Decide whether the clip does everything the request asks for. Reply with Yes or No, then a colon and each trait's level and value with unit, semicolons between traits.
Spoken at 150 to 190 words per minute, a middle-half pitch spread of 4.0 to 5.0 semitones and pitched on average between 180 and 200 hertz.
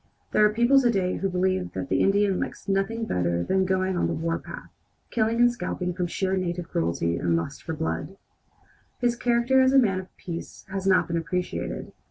No: average, 200 wpm; average, 4.3 semitones; high, 190 Hz